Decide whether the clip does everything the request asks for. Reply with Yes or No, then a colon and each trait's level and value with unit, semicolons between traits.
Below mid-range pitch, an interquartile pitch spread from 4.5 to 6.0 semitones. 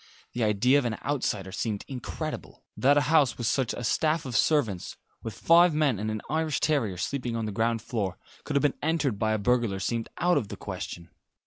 Yes: low, 120 Hz; average, 5.1 semitones